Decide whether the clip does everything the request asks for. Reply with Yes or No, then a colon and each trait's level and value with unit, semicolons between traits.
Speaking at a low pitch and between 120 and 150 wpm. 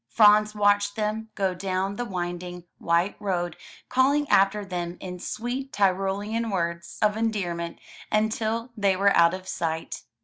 No: high, 200 Hz; average, 140 wpm